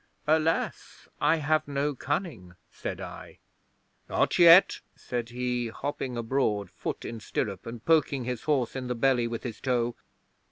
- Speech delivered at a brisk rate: No, average, 150 wpm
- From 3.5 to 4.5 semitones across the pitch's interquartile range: Yes, average, 3.8 semitones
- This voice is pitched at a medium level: No, low, 125 Hz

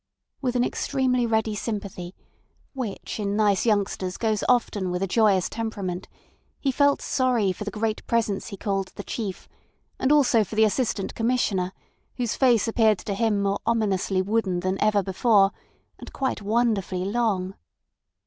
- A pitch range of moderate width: Yes, average, 3.1 semitones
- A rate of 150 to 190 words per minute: Yes, average, 155 wpm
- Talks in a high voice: Yes, high, 215 Hz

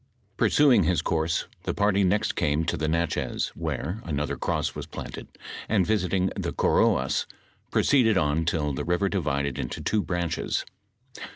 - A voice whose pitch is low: Yes, very low, 85 Hz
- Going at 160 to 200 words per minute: No, average, 150 wpm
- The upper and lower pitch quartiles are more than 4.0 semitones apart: Yes, average, 4.5 semitones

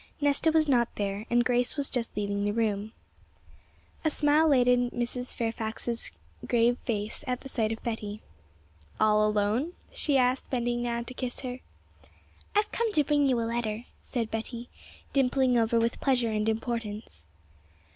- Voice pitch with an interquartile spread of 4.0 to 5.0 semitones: No, average, 2.7 semitones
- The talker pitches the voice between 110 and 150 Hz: No, high, 240 Hz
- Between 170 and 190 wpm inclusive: No, average, 155 wpm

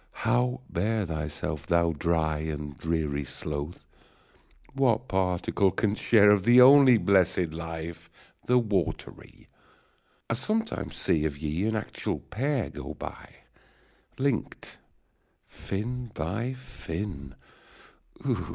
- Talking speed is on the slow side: Yes, slow, 105 wpm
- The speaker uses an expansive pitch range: Yes, wide, 7.0 semitones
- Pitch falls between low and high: No, very low, 95 Hz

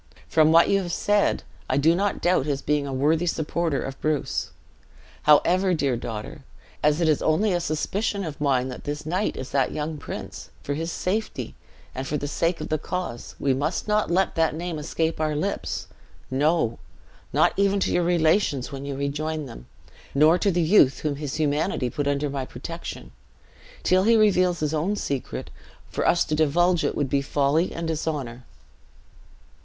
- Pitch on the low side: No, medium, 155 Hz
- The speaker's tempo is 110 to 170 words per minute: No, average, 180 wpm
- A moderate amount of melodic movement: Yes, average, 3.7 semitones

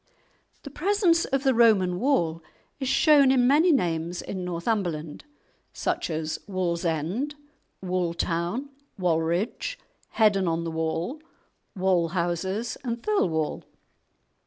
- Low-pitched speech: No, medium, 185 Hz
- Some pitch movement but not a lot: No, wide, 7.6 semitones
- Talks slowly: Yes, slow, 105 wpm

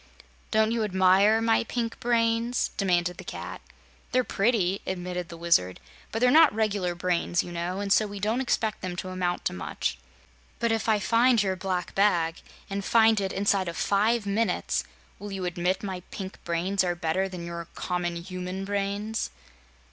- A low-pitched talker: No, high, 195 Hz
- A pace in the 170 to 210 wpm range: Yes, average, 175 wpm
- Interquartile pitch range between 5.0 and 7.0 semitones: No, average, 3.6 semitones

